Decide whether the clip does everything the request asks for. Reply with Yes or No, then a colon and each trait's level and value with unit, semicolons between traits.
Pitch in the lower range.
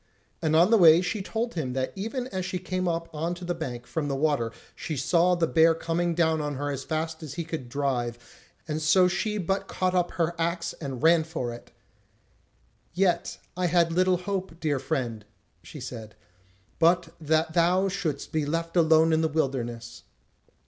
No: medium, 165 Hz